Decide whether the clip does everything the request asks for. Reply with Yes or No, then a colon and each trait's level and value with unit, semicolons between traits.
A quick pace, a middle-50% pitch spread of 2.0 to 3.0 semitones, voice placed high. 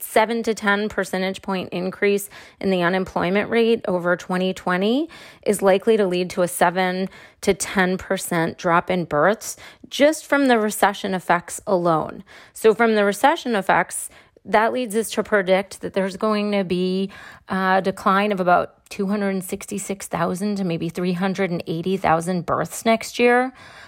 No: average, 145 wpm; average, 2.7 semitones; high, 195 Hz